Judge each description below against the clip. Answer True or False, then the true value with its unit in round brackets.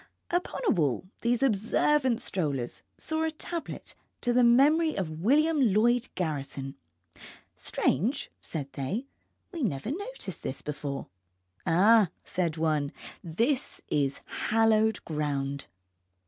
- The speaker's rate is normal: False (120 wpm)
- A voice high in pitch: True (215 Hz)